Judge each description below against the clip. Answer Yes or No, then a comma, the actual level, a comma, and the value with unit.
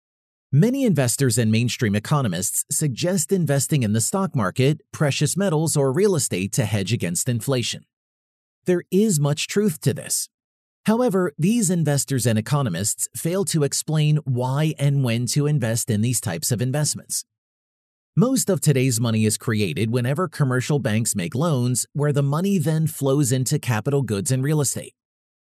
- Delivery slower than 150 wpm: No, average, 155 wpm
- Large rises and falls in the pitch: No, average, 4.4 semitones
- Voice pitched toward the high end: No, medium, 140 Hz